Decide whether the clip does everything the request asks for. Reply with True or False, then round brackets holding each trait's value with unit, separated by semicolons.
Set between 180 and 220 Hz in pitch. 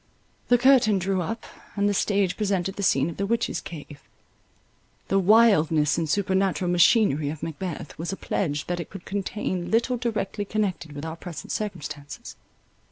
True (190 Hz)